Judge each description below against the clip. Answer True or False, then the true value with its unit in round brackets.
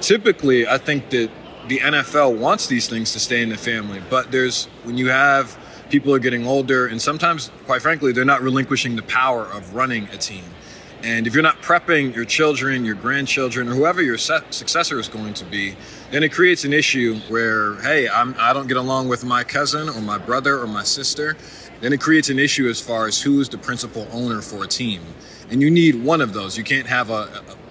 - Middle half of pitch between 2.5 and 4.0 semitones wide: True (3.7 semitones)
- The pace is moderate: False (225 wpm)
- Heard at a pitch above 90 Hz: True (125 Hz)